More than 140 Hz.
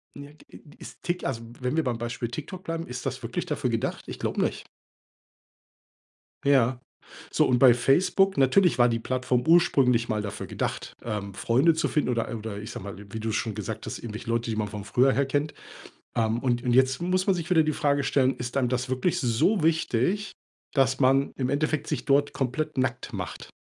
No: low, 130 Hz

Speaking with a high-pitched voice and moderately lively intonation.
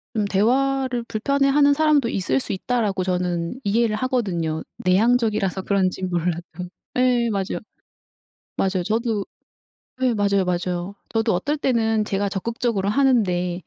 Yes: high, 210 Hz; average, 4.8 semitones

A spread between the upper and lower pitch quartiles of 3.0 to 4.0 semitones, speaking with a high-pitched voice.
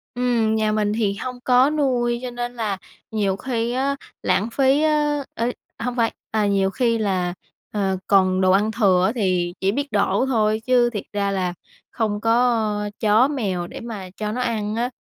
Yes: average, 3.6 semitones; high, 220 Hz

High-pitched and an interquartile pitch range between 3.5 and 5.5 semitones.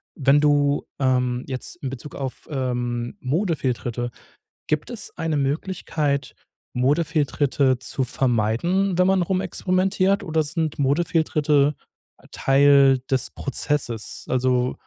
No: medium, 140 Hz; average, 4.1 semitones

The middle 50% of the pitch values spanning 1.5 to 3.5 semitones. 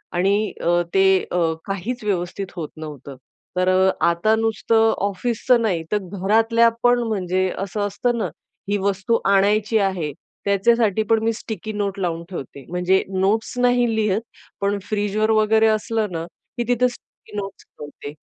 Yes: average, 3.1 semitones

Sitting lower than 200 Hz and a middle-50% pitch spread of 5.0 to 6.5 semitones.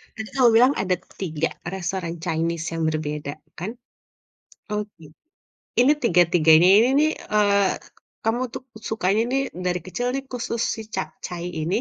Yes: medium, 185 Hz; average, 5.3 semitones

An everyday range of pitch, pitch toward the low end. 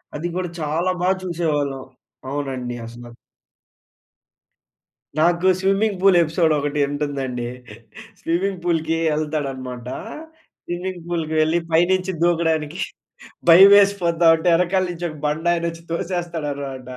No: average, 3.3 semitones; medium, 165 Hz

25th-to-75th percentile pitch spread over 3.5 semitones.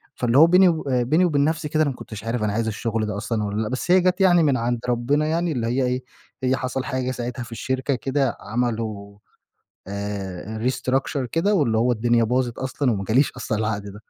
Yes: average, 4.2 semitones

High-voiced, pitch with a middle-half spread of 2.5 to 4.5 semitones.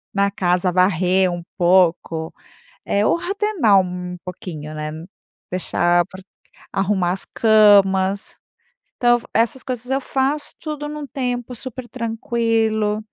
No: high, 205 Hz; average, 5.1 semitones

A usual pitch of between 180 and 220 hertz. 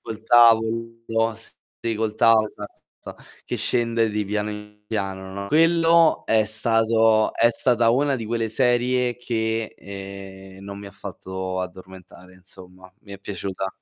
No: low, 110 Hz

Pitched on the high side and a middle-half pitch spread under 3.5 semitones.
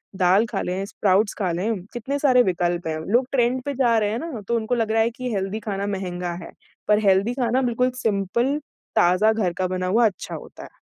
No: high, 215 Hz; average, 4.2 semitones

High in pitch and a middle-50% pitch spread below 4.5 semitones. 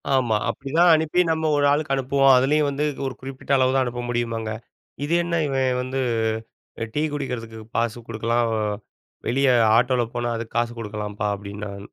No: low, 125 Hz; average, 3.2 semitones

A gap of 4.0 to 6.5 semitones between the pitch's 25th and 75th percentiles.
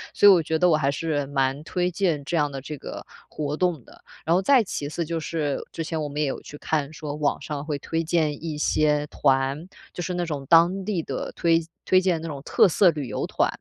No: average, 2.8 semitones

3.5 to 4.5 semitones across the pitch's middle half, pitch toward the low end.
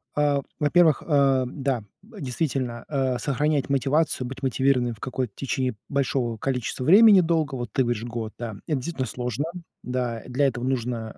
No: average, 2.9 semitones; low, 130 Hz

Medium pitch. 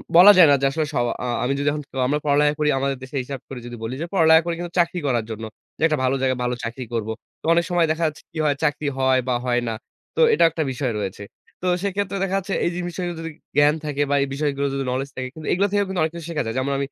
Yes: medium, 145 Hz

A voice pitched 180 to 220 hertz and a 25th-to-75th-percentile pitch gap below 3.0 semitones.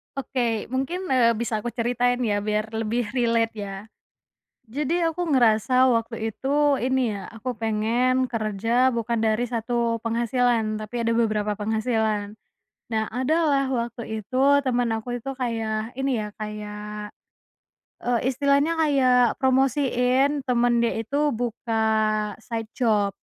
No: high, 235 Hz; narrow, 2.6 semitones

